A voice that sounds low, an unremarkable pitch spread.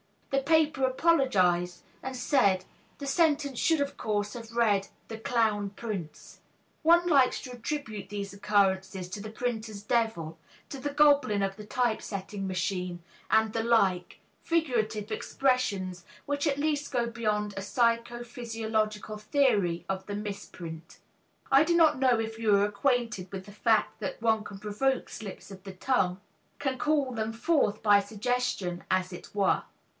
No: high, 220 Hz; average, 4.5 semitones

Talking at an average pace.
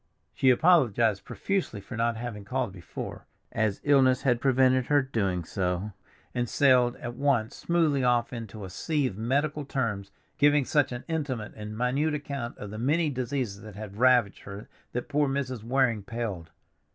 Yes: average, 165 wpm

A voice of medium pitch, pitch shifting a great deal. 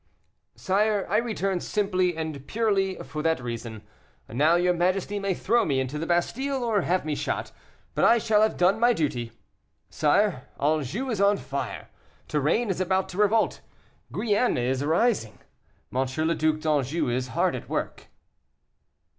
Yes: medium, 175 Hz; wide, 6.1 semitones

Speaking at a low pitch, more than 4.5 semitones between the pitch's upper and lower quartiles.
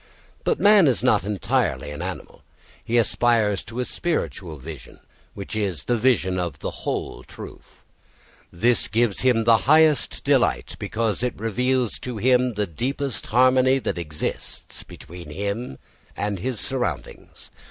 Yes: low, 115 Hz; average, 4.9 semitones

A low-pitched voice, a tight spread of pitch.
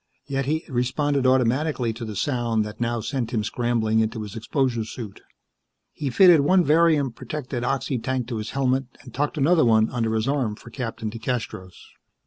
No: low, 125 Hz; average, 3.6 semitones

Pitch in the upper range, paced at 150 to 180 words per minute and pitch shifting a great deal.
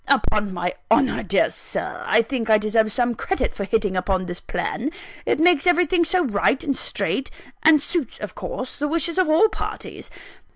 No: very high, 255 Hz; average, 190 wpm; wide, 7.2 semitones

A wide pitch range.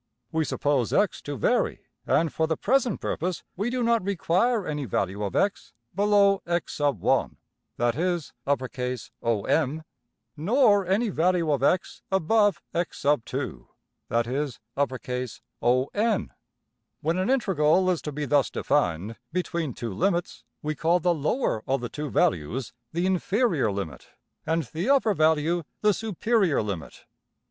Yes: wide, 6.8 semitones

